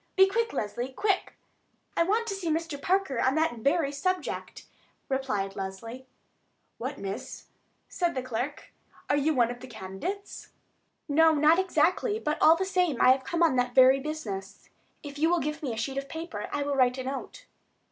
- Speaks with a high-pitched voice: Yes, very high, 285 Hz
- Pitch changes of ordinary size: Yes, average, 5.0 semitones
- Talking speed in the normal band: Yes, average, 185 wpm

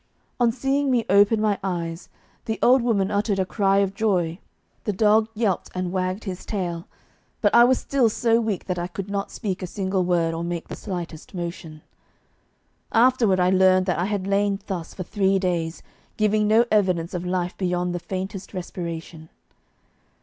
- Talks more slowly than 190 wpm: Yes, average, 180 wpm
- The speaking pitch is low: No, high, 190 Hz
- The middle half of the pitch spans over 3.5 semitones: No, average, 3.2 semitones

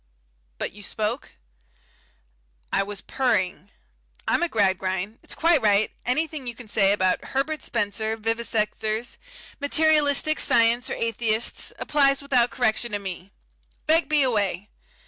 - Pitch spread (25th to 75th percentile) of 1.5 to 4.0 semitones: No, average, 5.0 semitones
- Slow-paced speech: Yes, slow, 125 wpm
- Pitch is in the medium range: No, high, 230 Hz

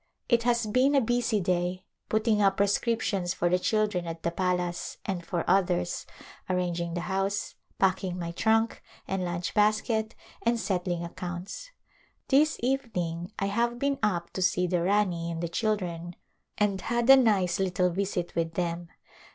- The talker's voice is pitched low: No, high, 190 Hz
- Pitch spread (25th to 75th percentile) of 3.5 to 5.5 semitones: Yes, average, 3.9 semitones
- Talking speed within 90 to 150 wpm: No, average, 165 wpm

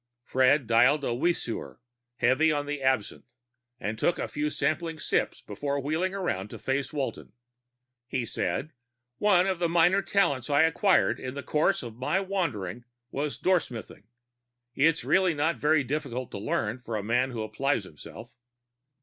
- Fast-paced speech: No, average, 160 wpm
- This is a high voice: No, medium, 140 Hz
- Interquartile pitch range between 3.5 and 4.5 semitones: No, average, 5.3 semitones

